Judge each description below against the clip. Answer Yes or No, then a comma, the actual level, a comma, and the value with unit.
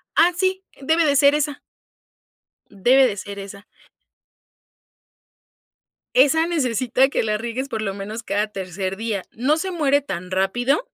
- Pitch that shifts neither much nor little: No, wide, 6.5 semitones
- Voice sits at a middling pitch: No, high, 245 Hz